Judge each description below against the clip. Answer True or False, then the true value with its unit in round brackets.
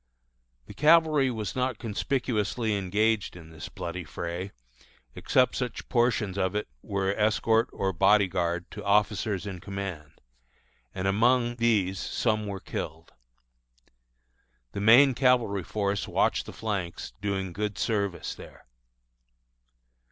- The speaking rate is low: True (125 wpm)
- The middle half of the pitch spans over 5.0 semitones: False (3.2 semitones)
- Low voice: True (105 Hz)